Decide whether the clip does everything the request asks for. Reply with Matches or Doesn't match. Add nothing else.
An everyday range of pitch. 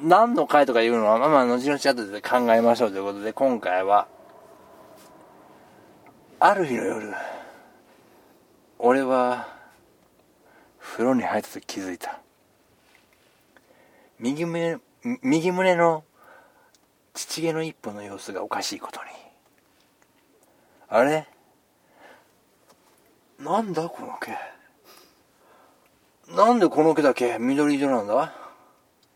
Doesn't match